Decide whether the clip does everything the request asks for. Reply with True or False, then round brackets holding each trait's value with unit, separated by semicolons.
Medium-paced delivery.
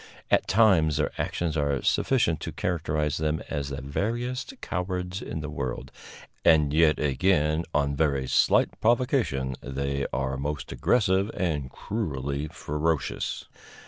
False (130 wpm)